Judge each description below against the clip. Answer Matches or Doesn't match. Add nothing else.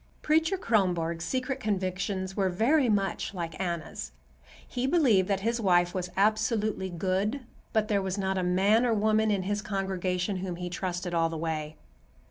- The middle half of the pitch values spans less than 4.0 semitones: Matches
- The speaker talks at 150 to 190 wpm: Matches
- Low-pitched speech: Doesn't match